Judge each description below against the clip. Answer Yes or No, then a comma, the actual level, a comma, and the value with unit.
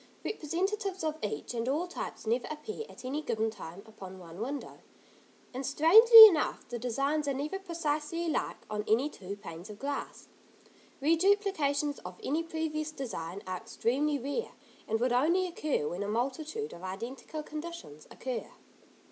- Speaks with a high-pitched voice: Yes, very high, 285 Hz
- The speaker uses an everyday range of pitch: No, wide, 6.5 semitones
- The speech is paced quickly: No, average, 155 wpm